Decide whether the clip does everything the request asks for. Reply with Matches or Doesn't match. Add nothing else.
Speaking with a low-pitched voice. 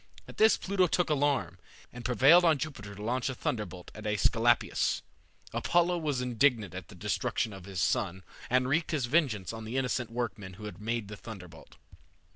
Matches